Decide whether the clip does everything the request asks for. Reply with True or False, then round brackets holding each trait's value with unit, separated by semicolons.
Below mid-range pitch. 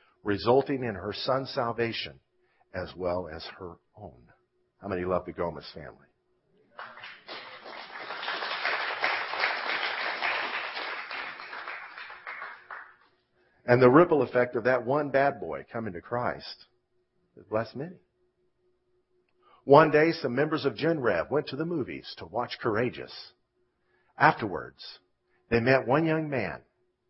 True (130 Hz)